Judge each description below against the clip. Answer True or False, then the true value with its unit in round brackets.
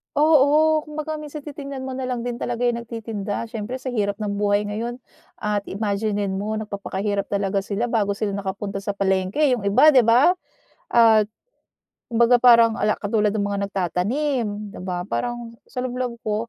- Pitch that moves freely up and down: False (3.8 semitones)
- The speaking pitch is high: True (220 Hz)